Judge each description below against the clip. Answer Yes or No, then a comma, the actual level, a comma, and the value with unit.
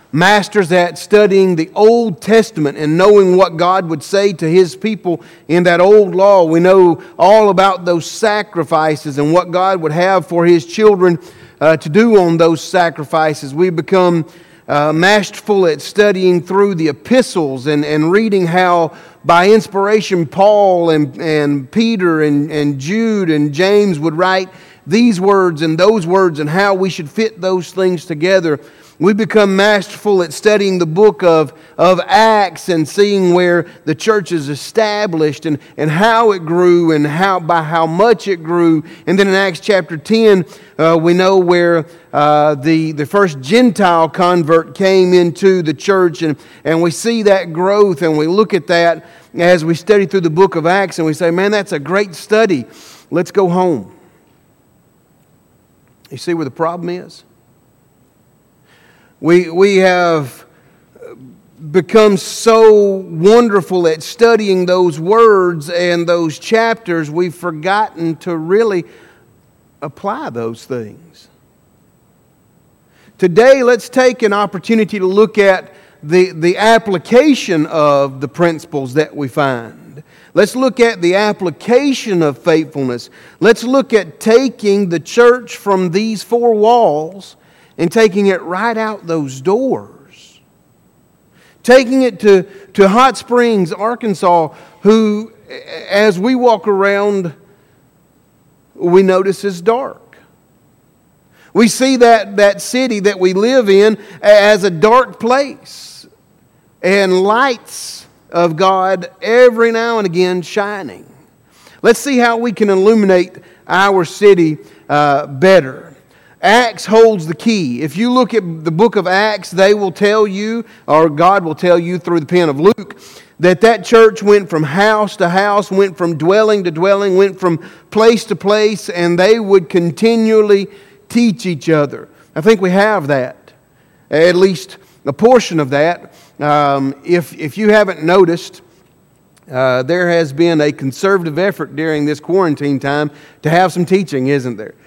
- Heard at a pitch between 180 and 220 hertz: Yes, medium, 185 Hz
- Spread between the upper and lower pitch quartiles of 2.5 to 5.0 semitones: Yes, average, 4.0 semitones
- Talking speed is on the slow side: No, average, 150 wpm